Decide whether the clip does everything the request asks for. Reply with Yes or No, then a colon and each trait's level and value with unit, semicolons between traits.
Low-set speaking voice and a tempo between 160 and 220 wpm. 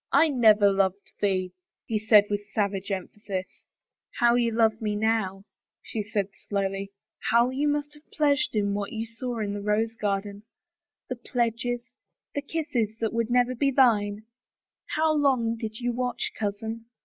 No: high, 225 Hz; average, 165 wpm